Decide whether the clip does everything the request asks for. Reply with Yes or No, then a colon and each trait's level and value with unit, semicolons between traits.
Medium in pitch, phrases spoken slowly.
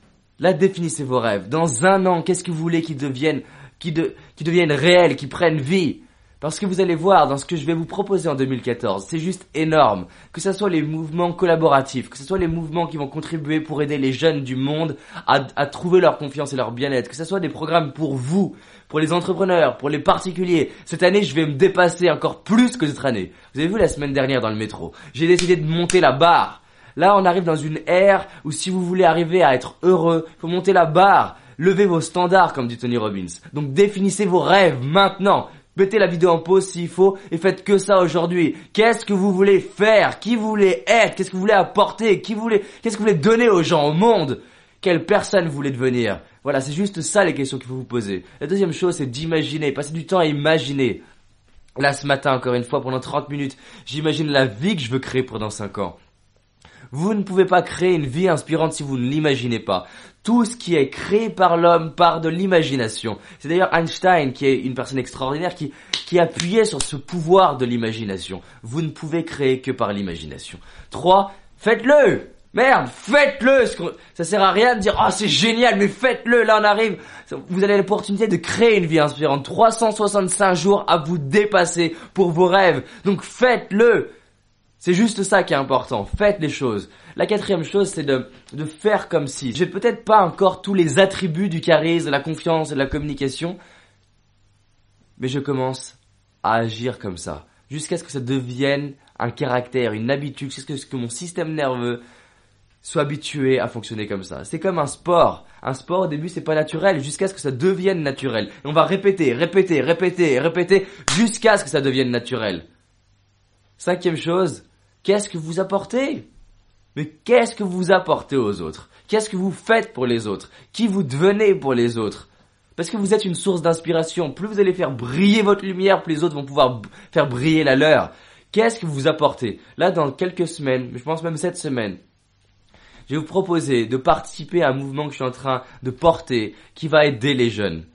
No: medium, 160 Hz; average, 205 wpm